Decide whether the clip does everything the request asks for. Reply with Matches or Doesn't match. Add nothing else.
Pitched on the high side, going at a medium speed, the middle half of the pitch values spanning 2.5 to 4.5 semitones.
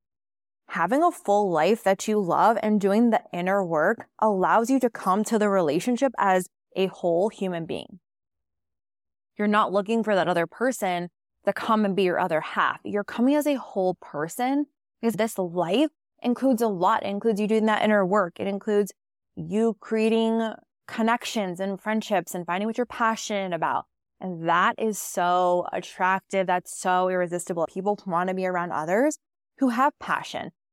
Matches